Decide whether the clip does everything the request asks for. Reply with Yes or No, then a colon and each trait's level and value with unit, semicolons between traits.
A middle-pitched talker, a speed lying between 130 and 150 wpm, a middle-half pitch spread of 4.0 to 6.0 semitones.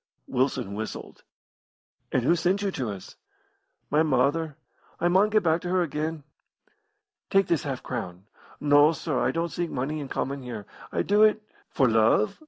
No: medium, 150 Hz; average, 175 wpm; average, 5.2 semitones